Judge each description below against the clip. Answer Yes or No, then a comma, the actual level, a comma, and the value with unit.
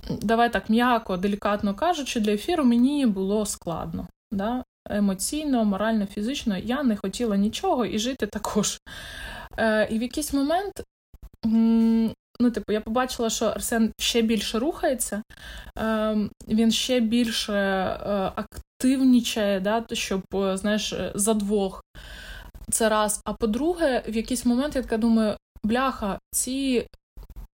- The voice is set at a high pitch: Yes, high, 225 Hz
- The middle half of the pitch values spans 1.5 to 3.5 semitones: Yes, average, 2.8 semitones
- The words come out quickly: No, average, 125 wpm